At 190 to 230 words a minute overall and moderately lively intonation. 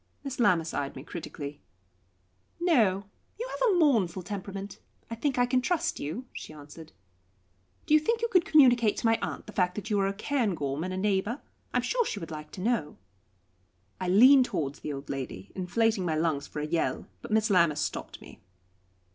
No: average, 195 wpm; wide, 7.5 semitones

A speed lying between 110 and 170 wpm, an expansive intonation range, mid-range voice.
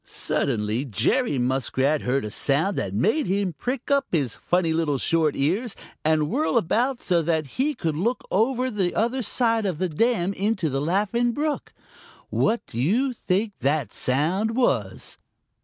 Yes: average, 160 wpm; wide, 7.9 semitones; medium, 180 Hz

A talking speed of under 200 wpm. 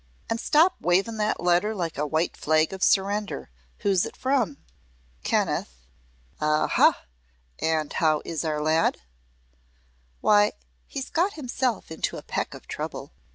Yes: slow, 135 wpm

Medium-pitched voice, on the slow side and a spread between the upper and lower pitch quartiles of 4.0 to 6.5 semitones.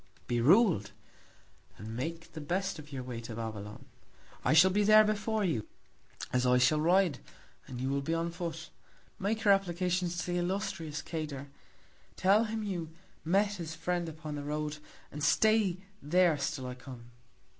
No: medium, 165 Hz; average, 165 wpm; average, 5.3 semitones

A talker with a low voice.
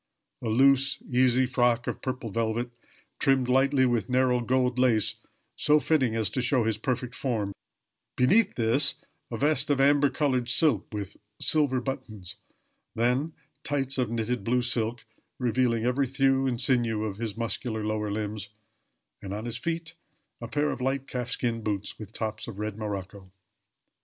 Yes: low, 125 Hz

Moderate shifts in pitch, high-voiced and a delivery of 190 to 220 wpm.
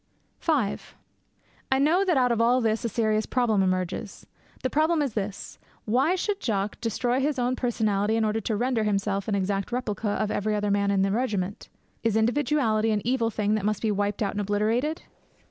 Yes: average, 3.6 semitones; high, 220 Hz; average, 195 wpm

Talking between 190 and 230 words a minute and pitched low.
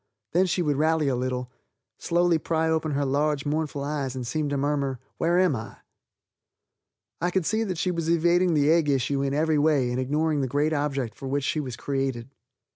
No: average, 200 wpm; medium, 150 Hz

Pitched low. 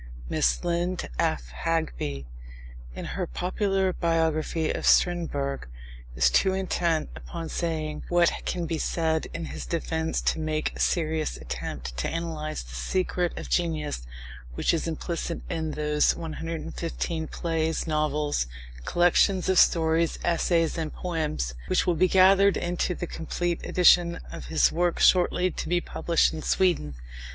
No: medium, 165 Hz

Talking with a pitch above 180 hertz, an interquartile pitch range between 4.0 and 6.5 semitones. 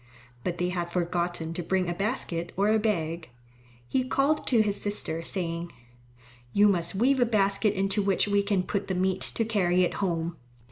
No: high, 190 Hz; average, 3.2 semitones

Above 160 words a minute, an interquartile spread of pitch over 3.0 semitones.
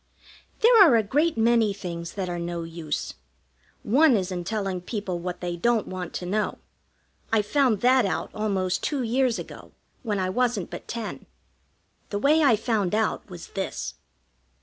Yes: average, 170 wpm; average, 4.7 semitones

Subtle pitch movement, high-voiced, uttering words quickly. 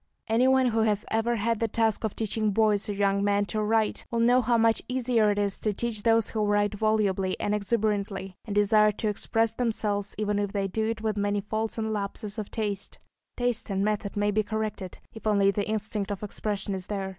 Yes: narrow, 1.6 semitones; high, 215 Hz; fast, 215 wpm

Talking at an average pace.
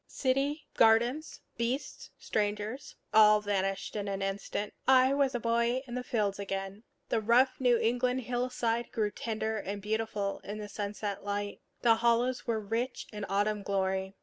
Yes: average, 150 wpm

